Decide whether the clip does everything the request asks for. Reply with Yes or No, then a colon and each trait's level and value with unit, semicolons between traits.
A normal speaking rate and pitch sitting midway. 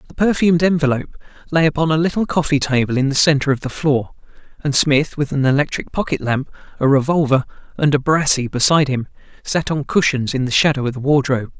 Yes: average, 195 wpm; medium, 145 Hz